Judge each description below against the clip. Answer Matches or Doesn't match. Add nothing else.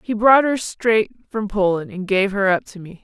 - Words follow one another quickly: Matches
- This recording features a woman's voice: Matches